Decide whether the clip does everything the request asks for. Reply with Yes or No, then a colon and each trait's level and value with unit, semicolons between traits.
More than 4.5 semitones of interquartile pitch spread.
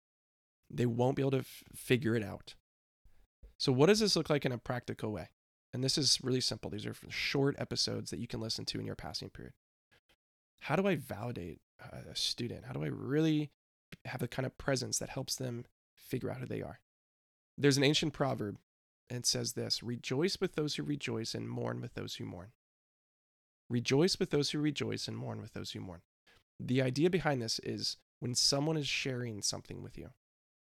Yes: average, 4.9 semitones